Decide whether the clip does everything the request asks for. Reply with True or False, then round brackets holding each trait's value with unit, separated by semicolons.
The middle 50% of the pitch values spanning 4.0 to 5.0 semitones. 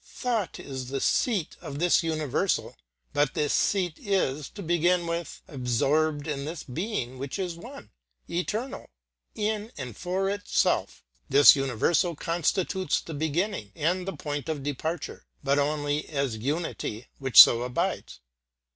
True (4.6 semitones)